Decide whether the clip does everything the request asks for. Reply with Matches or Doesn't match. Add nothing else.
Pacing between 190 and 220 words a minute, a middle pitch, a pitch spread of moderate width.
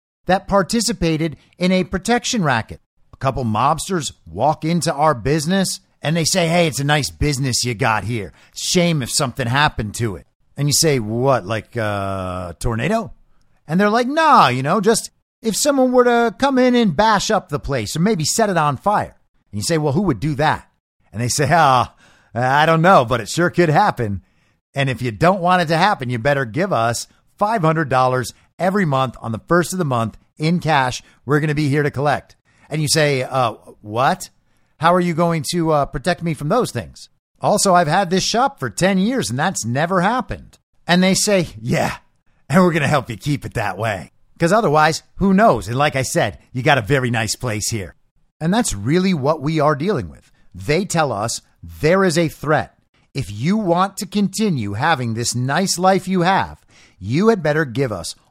Doesn't match